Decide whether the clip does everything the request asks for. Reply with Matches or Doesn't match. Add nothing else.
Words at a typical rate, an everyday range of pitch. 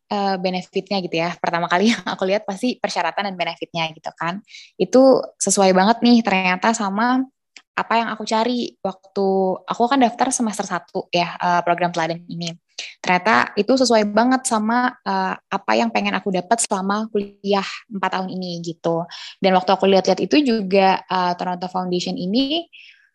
Doesn't match